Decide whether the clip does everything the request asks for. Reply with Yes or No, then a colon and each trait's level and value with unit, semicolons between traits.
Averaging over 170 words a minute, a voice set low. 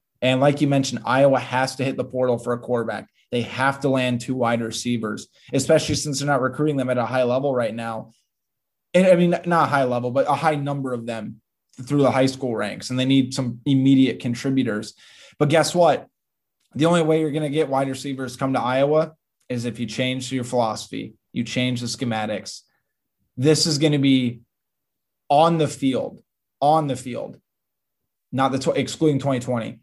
Yes: average, 195 wpm; low, 130 Hz